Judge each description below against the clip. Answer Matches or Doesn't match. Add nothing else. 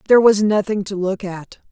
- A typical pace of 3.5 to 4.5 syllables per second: Doesn't match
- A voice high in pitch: Matches